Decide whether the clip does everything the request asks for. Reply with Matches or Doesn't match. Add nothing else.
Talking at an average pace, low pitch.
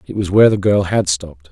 Doesn't match